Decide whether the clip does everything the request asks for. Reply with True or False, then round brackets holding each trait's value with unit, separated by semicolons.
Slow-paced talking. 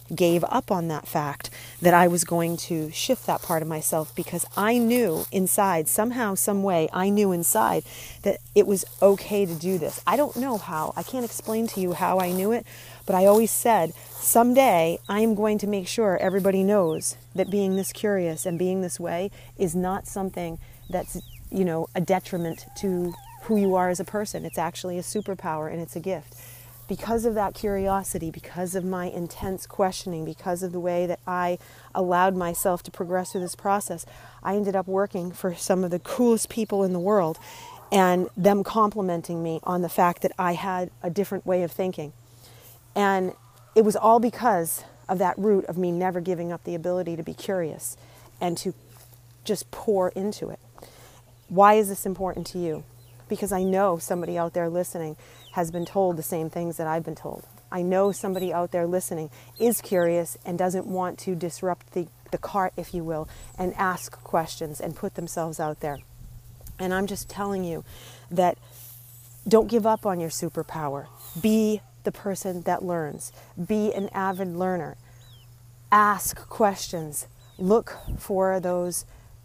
False (180 wpm)